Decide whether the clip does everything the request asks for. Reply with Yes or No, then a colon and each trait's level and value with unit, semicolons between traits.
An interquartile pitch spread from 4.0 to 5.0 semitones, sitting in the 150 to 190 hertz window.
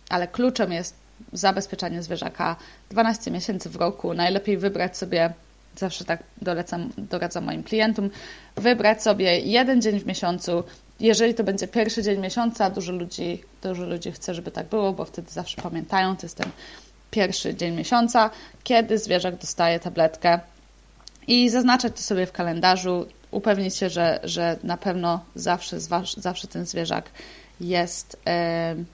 No: average, 3.6 semitones; medium, 185 Hz